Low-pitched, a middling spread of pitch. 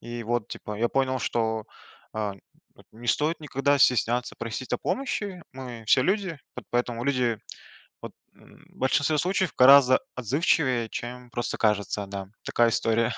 Yes: low, 125 Hz; average, 3.5 semitones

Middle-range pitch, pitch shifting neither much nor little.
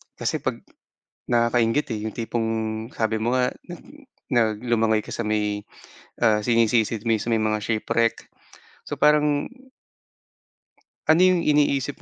No: low, 115 Hz; average, 3.1 semitones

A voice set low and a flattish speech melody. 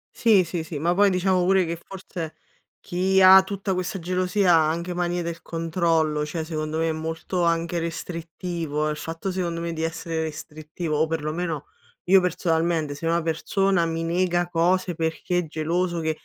No: medium, 170 Hz; narrow, 2.0 semitones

